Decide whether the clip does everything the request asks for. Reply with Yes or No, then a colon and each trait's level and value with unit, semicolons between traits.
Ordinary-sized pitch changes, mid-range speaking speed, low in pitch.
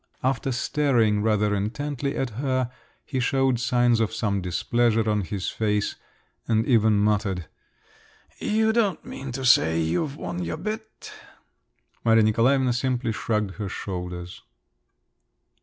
No: average, 4.2 semitones; slow, 125 wpm; low, 115 Hz